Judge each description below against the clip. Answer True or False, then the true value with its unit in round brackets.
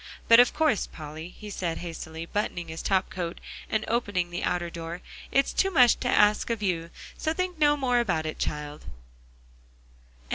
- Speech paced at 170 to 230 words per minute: True (175 wpm)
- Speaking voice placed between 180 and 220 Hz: True (185 Hz)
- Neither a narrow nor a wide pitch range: False (6.3 semitones)